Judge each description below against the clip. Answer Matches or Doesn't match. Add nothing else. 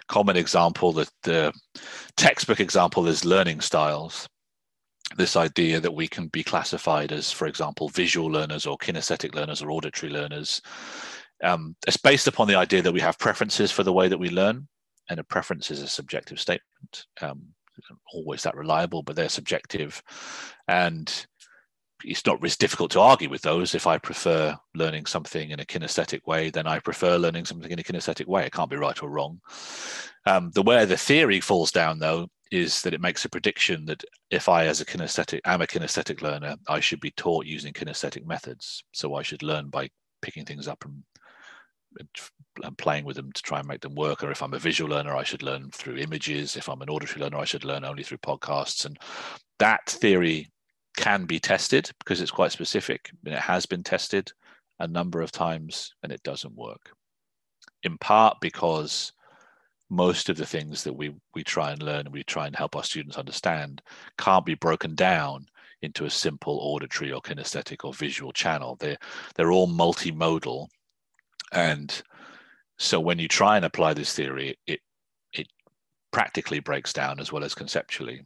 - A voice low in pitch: Matches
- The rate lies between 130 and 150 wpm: Doesn't match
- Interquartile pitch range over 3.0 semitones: Doesn't match